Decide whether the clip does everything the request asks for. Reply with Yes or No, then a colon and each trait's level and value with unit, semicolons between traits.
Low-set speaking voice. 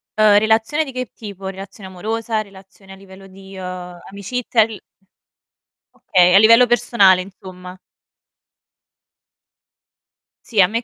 No: high, 195 Hz